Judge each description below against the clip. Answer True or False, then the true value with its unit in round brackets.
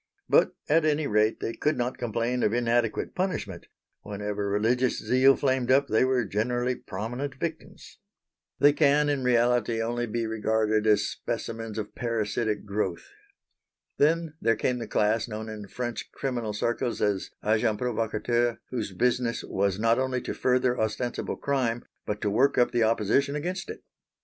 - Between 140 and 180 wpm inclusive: True (155 wpm)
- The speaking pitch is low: True (120 Hz)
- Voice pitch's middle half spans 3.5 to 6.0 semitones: False (3.1 semitones)